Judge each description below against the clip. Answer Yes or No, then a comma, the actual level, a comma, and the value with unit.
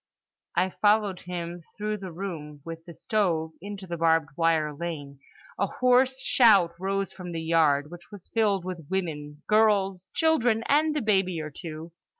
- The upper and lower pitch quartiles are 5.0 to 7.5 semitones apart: No, average, 4.1 semitones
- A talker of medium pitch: Yes, medium, 180 Hz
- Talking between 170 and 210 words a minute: No, average, 155 wpm